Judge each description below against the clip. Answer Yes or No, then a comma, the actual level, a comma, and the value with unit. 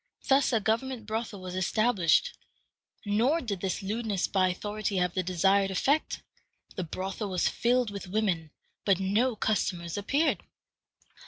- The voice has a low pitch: No, high, 205 Hz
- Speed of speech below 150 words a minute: Yes, average, 140 wpm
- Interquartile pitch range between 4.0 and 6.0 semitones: No, average, 3.5 semitones